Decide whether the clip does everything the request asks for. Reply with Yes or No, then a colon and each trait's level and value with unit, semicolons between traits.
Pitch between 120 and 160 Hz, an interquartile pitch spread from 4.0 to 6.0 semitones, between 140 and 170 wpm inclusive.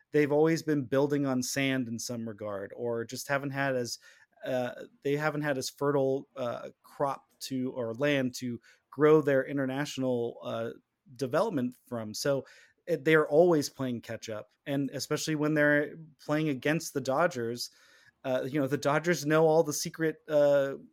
No: medium, 140 Hz; average, 3.0 semitones; average, 160 wpm